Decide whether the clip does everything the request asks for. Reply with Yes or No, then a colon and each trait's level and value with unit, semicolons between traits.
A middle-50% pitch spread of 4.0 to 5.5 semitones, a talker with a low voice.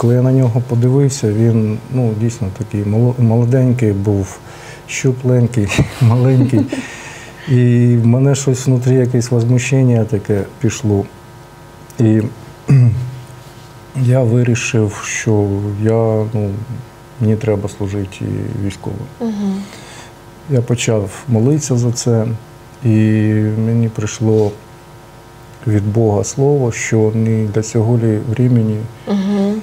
No: narrow, 2.5 semitones; low, 120 Hz